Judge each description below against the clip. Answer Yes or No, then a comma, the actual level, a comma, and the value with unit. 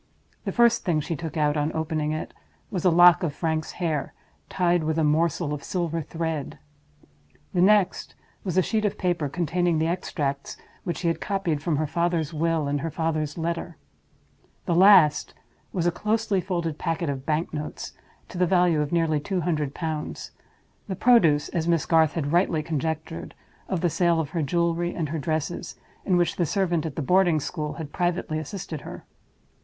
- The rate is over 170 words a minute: Yes, average, 180 wpm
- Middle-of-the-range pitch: Yes, medium, 165 Hz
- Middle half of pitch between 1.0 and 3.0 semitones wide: Yes, narrow, 2.4 semitones